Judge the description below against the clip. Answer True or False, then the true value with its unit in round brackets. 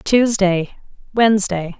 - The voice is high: True (200 Hz)